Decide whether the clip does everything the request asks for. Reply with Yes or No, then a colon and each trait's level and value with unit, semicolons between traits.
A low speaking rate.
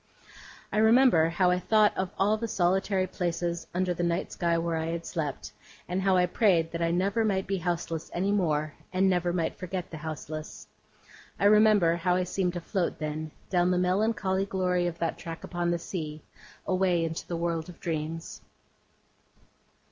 No: average, 180 wpm